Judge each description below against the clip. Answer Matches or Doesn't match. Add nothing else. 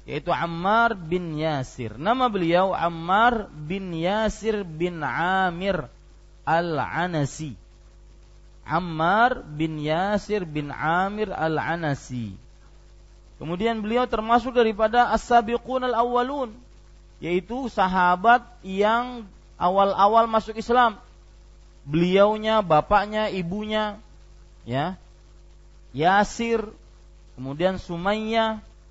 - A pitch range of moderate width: Doesn't match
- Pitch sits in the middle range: Matches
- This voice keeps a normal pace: Doesn't match